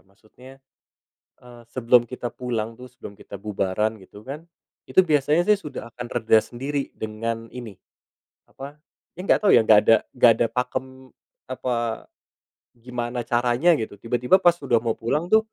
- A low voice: Yes, low, 120 Hz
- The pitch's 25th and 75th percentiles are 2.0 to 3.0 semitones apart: Yes, average, 2.7 semitones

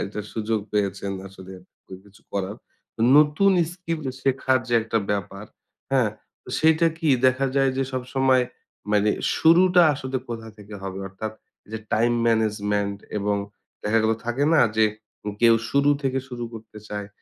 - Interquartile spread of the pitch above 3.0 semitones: Yes, average, 4.5 semitones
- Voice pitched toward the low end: Yes, low, 115 Hz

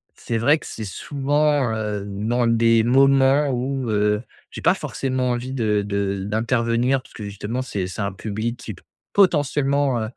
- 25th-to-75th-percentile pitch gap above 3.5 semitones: Yes, average, 4.2 semitones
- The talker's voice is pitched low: Yes, low, 120 Hz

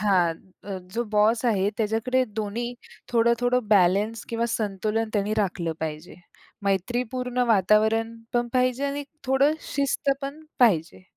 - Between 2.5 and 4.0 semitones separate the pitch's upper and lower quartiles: Yes, average, 3.7 semitones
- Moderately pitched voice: No, high, 225 Hz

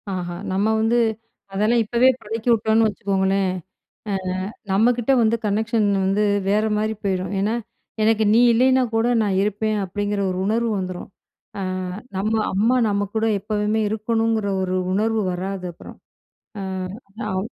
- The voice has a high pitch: Yes, high, 210 Hz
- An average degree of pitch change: No, narrow, 2.3 semitones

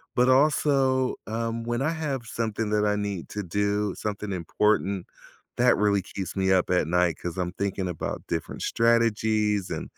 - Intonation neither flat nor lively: Yes, average, 3.5 semitones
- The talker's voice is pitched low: Yes, low, 105 Hz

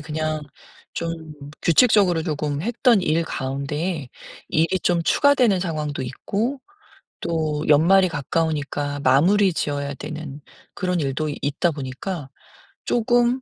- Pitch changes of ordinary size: Yes, average, 4.3 semitones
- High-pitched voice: No, medium, 160 Hz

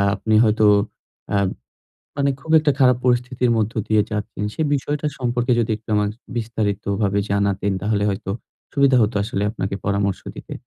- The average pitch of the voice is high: No, low, 110 Hz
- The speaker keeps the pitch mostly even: No, average, 3.6 semitones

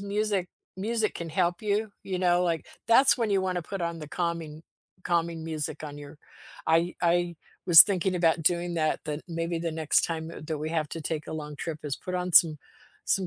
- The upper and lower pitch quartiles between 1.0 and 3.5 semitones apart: Yes, narrow, 2.4 semitones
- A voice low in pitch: No, medium, 170 Hz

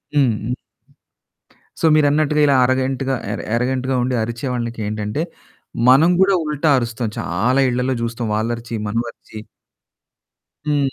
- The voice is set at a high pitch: No, low, 125 Hz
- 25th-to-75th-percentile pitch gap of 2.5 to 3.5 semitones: Yes, average, 3.1 semitones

